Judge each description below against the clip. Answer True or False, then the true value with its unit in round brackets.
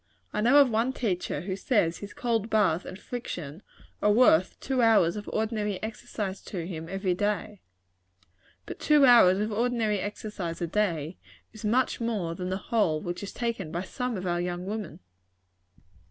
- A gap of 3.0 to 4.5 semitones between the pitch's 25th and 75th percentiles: True (4.1 semitones)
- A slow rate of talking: False (170 wpm)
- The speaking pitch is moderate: False (205 Hz)